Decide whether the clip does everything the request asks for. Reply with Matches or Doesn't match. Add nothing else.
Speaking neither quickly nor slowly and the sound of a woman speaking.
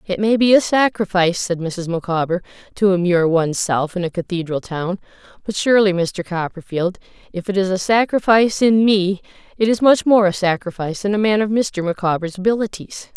Matches